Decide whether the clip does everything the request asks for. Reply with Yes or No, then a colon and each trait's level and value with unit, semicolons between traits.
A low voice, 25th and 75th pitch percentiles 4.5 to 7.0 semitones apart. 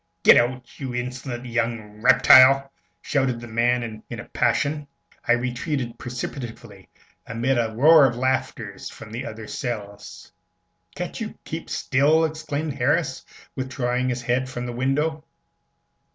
No: low, 125 Hz; narrow, 2.4 semitones